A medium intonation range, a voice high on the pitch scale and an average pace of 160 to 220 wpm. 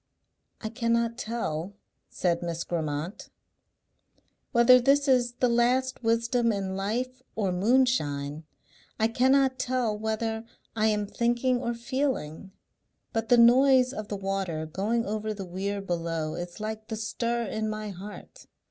No: average, 3.8 semitones; high, 220 Hz; average, 140 wpm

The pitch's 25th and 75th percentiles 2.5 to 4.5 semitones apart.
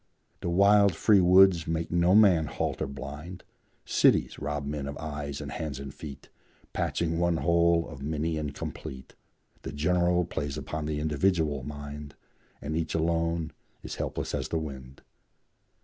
Yes: average, 2.9 semitones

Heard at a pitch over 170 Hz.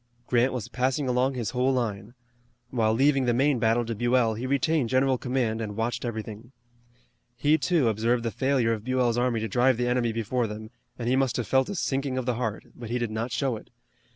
No: low, 120 Hz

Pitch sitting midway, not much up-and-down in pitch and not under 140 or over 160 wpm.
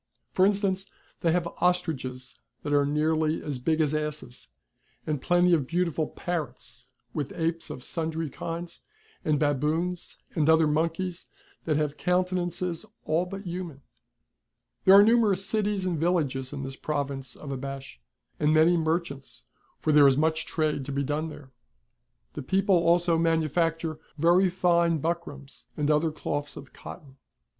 No: medium, 160 Hz; average, 3.2 semitones; average, 150 wpm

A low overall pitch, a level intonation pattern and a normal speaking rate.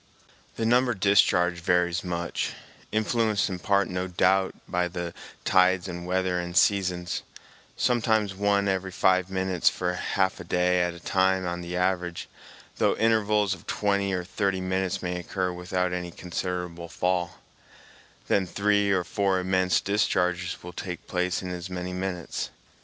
Yes: very low, 90 Hz; narrow, 1.6 semitones; average, 150 wpm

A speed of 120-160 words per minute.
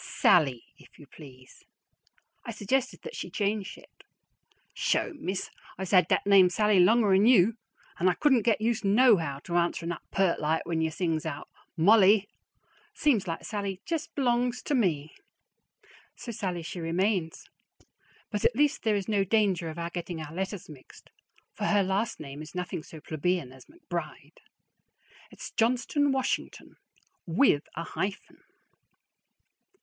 Yes: average, 150 wpm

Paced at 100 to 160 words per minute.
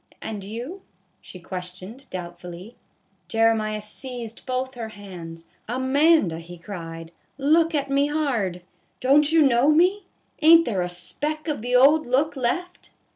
Yes: average, 145 wpm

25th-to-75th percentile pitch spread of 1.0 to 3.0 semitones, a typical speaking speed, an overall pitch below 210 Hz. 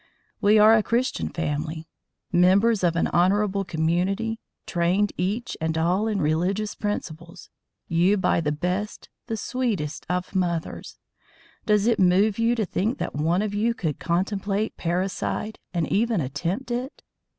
No: average, 4.0 semitones; average, 145 wpm; high, 190 Hz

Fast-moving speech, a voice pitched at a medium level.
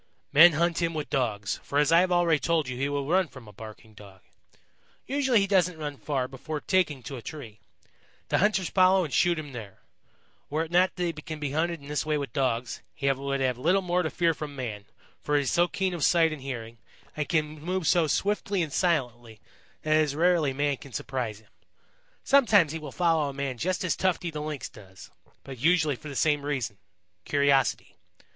Yes: fast, 210 wpm; medium, 150 Hz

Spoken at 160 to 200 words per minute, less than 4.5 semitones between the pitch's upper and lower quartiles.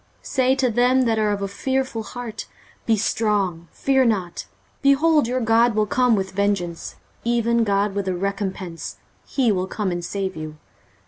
Yes: average, 175 wpm; average, 4.1 semitones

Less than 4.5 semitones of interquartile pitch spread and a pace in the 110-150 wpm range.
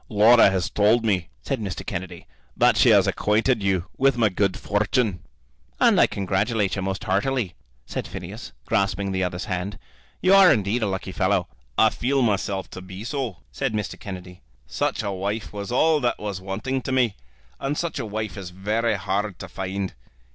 No: average, 3.7 semitones; average, 185 wpm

